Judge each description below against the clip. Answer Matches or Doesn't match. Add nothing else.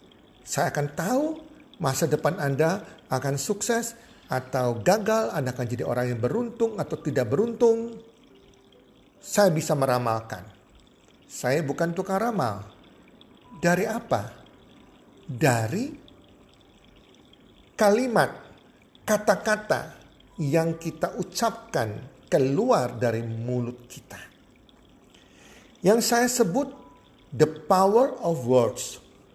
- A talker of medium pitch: Matches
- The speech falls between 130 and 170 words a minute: Doesn't match